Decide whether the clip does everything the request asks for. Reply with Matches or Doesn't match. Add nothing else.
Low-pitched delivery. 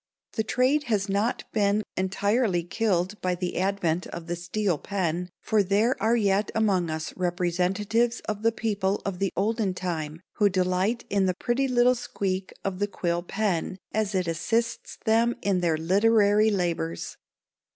Doesn't match